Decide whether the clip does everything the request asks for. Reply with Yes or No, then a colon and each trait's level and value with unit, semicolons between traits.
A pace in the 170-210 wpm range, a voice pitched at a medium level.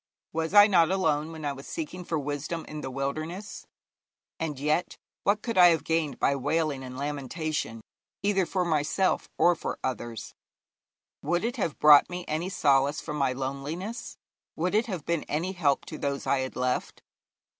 Yes: average, 175 wpm; medium, 155 Hz